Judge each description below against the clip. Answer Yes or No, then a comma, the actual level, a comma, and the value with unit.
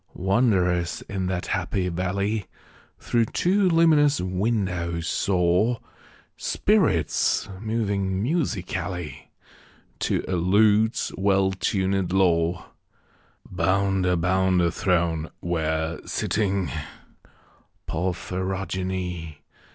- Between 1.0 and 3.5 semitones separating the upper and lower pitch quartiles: Yes, narrow, 2.5 semitones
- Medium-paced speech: No, slow, 80 wpm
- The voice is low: Yes, very low, 95 Hz